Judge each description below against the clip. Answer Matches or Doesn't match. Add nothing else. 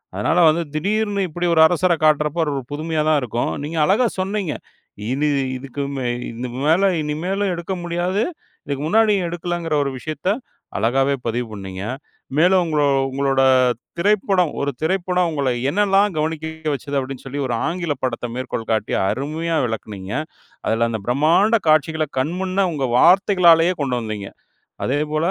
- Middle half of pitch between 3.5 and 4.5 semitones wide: Doesn't match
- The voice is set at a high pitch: Doesn't match